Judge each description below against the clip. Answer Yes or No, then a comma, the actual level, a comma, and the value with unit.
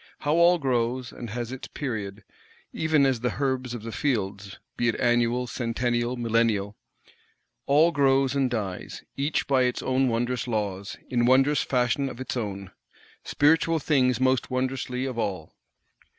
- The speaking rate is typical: Yes, average, 150 wpm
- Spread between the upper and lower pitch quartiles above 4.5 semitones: No, average, 2.7 semitones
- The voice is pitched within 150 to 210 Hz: No, low, 125 Hz